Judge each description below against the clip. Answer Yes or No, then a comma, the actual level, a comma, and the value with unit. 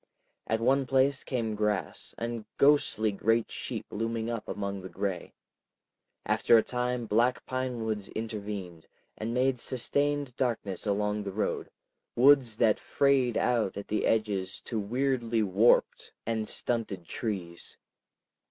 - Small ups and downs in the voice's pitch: No, average, 3.1 semitones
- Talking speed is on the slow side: Yes, slow, 130 wpm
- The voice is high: No, low, 115 Hz